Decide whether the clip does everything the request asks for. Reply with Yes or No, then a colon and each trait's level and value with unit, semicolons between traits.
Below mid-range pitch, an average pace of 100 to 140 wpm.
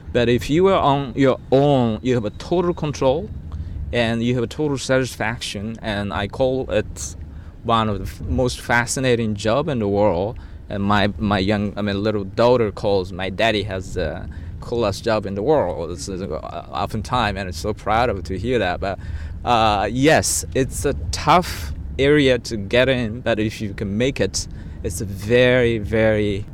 No: low, 105 Hz; average, 190 wpm